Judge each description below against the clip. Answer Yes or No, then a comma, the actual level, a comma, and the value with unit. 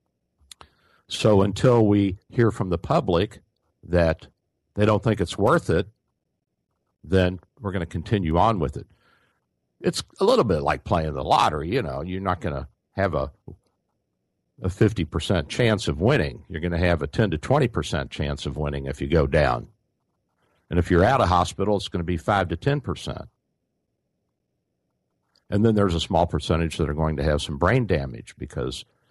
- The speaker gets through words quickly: No, average, 175 wpm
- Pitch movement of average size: Yes, average, 4.8 semitones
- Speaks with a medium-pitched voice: No, very low, 85 Hz